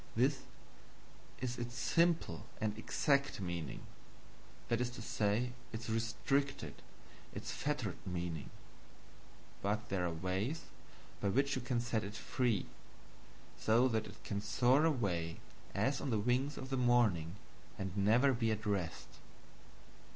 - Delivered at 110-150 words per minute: Yes, slow, 135 wpm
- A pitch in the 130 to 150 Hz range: No, low, 115 Hz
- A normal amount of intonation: Yes, average, 4.3 semitones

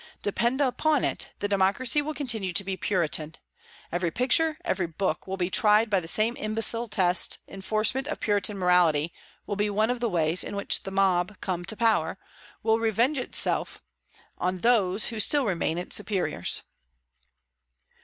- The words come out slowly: No, average, 165 wpm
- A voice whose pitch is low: No, high, 205 Hz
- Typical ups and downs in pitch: Yes, average, 4.2 semitones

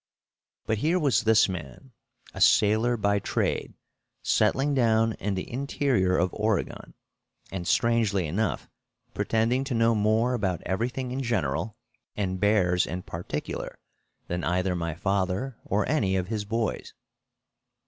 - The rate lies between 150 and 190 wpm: No, slow, 135 wpm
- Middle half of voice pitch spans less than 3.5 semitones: No, average, 4.0 semitones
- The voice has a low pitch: Yes, low, 105 Hz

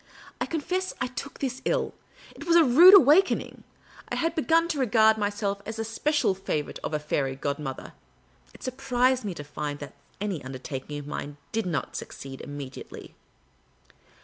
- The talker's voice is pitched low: No, high, 220 Hz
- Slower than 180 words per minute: Yes, average, 165 wpm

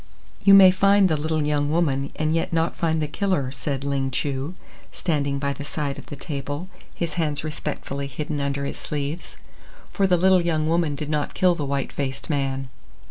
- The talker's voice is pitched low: No, medium, 150 Hz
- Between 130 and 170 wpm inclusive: No, average, 190 wpm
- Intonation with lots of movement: No, average, 3.0 semitones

